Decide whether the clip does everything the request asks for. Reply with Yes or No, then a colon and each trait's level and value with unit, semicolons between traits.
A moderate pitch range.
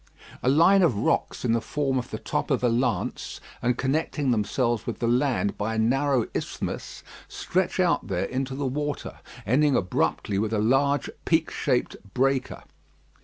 Yes: average, 3.6 semitones